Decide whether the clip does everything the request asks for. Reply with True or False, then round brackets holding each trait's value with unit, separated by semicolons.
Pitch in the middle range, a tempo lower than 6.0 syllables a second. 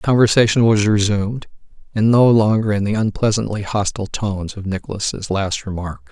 False (105 Hz; 5.5 syllables/s)